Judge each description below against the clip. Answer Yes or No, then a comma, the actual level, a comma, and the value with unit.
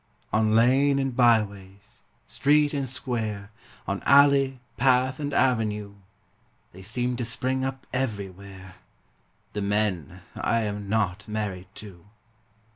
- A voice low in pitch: Yes, low, 110 Hz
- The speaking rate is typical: No, slow, 120 wpm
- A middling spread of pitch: Yes, average, 4.6 semitones